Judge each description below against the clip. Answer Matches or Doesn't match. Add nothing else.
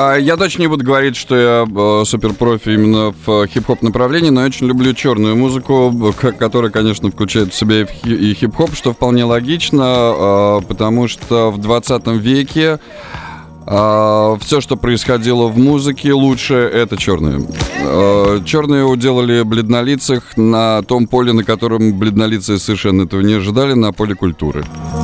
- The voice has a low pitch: Matches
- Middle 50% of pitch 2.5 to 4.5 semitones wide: Matches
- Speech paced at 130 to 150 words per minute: Matches